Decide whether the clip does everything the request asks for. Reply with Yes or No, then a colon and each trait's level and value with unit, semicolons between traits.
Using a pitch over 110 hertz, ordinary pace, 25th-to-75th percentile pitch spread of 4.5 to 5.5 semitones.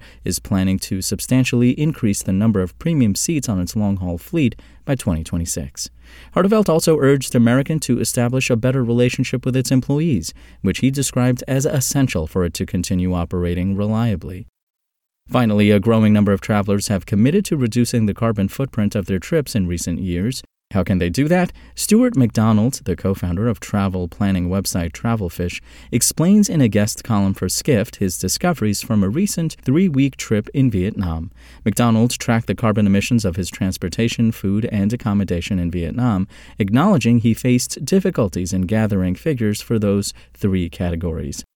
No: low, 105 Hz; average, 165 wpm; average, 5.2 semitones